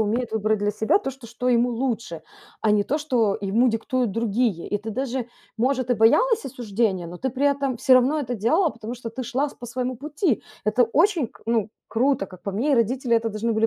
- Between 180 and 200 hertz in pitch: No, high, 235 Hz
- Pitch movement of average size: Yes, average, 3.2 semitones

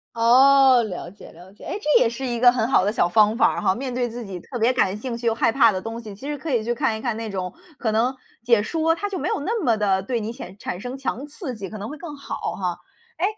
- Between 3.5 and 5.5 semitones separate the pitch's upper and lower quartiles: Yes, average, 4.1 semitones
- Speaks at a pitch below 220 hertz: No, high, 235 Hz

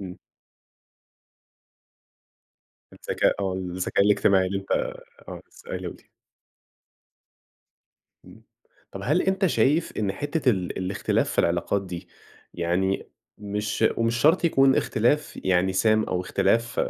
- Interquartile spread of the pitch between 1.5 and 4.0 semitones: No, average, 4.8 semitones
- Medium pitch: No, low, 100 Hz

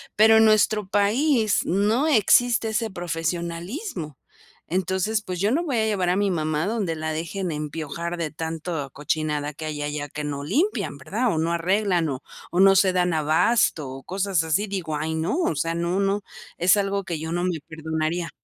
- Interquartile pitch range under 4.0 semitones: No, average, 4.4 semitones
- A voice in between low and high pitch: Yes, medium, 175 Hz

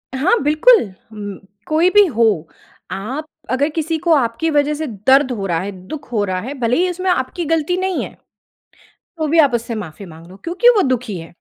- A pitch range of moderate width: No, wide, 7.2 semitones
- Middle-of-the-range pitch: No, very high, 285 Hz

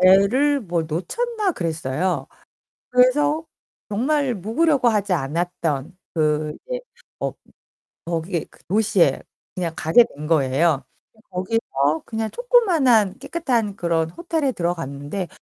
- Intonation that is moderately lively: No, wide, 7.8 semitones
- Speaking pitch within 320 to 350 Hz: No, high, 190 Hz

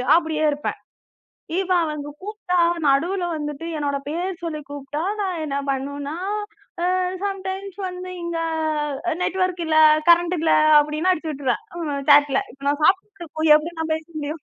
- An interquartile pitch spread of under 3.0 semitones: No, average, 3.7 semitones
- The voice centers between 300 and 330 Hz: Yes, very high, 320 Hz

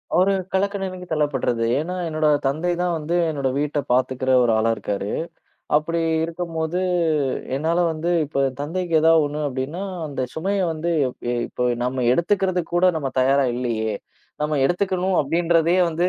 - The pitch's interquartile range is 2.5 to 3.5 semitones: No, average, 4.3 semitones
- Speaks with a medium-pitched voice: Yes, medium, 160 Hz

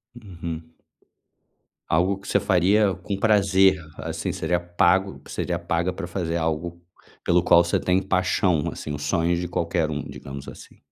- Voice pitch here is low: Yes, very low, 85 Hz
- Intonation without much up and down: Yes, narrow, 2.3 semitones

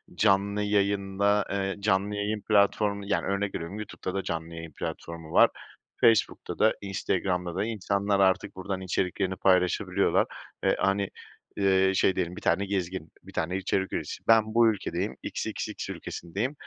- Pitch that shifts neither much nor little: No, narrow, 1.7 semitones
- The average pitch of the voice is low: Yes, very low, 95 Hz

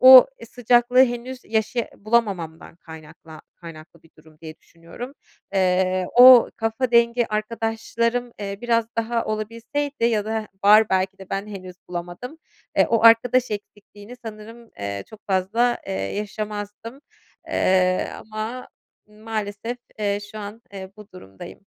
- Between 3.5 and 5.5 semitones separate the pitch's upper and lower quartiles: Yes, average, 3.8 semitones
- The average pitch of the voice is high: Yes, high, 215 Hz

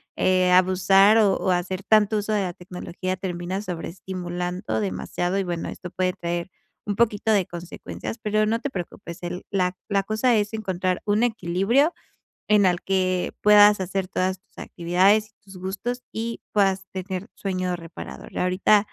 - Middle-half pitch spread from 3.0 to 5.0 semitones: No, narrow, 2.6 semitones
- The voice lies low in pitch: No, high, 190 Hz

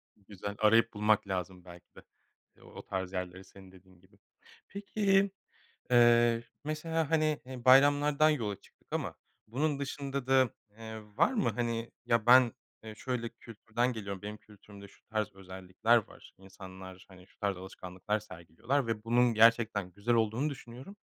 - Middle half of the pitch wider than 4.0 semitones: Yes, average, 5.0 semitones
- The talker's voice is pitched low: Yes, low, 115 Hz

